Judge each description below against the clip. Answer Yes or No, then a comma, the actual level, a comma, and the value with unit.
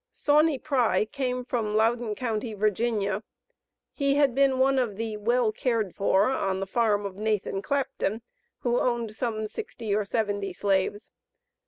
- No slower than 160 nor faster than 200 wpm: No, average, 150 wpm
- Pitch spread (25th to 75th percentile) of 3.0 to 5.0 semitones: Yes, average, 3.5 semitones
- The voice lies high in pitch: Yes, high, 225 Hz